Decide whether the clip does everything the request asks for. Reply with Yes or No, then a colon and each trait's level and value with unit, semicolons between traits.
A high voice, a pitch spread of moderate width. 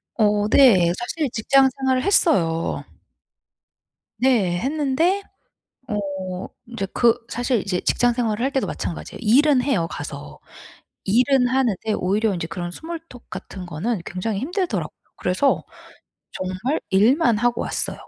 No: high, 235 Hz; wide, 5.8 semitones